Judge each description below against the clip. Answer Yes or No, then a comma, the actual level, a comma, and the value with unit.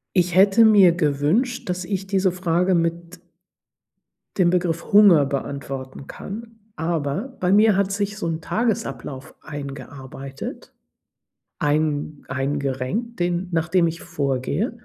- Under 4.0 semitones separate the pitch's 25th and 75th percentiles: No, average, 5.2 semitones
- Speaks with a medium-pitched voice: Yes, medium, 170 Hz